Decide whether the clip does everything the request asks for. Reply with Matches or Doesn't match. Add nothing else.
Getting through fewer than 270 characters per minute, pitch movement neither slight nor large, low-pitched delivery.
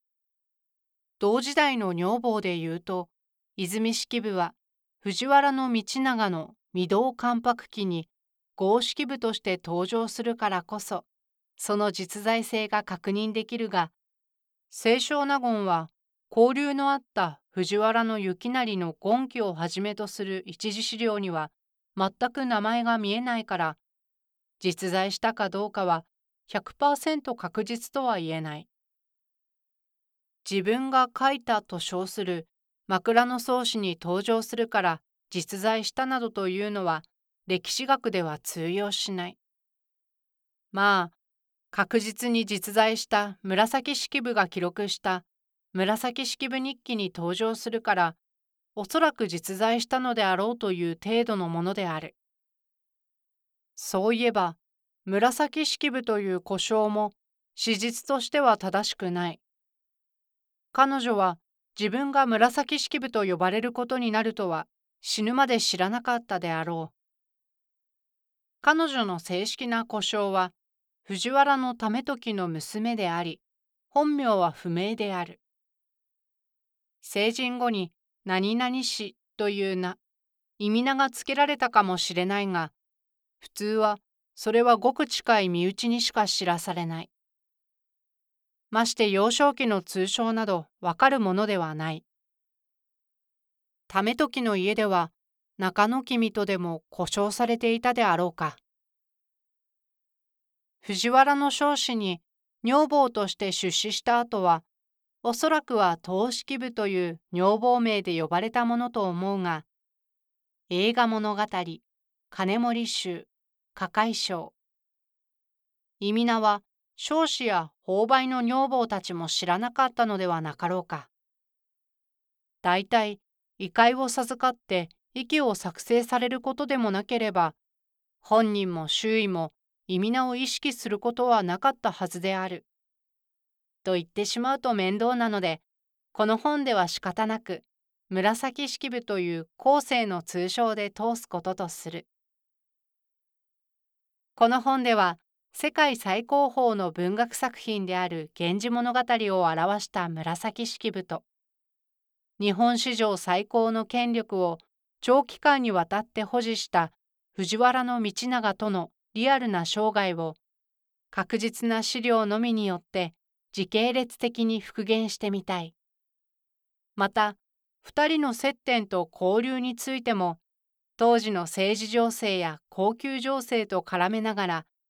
Doesn't match